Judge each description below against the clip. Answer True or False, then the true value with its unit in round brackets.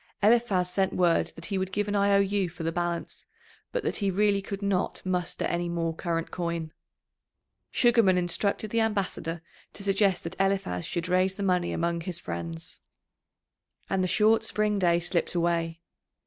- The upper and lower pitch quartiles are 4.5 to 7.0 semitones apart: False (2.8 semitones)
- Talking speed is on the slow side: False (175 wpm)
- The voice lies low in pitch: False (185 Hz)